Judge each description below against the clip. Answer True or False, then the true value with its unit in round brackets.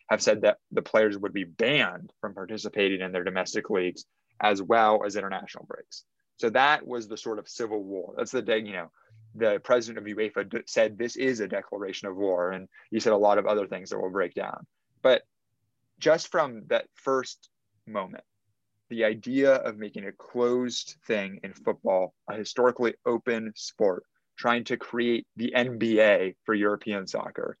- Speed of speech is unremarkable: True (180 wpm)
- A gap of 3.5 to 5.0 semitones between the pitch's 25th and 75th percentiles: False (2.9 semitones)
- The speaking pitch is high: False (110 Hz)